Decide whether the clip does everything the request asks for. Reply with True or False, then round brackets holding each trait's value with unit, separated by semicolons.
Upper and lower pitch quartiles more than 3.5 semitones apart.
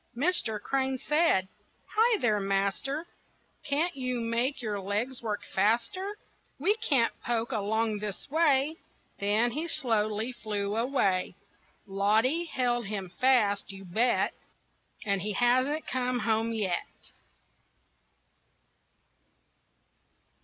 True (4.6 semitones)